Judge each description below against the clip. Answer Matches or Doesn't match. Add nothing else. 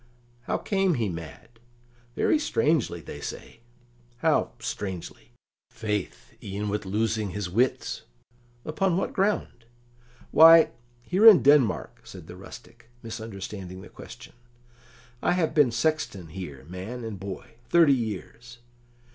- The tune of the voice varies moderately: Doesn't match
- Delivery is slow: Matches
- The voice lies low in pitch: Matches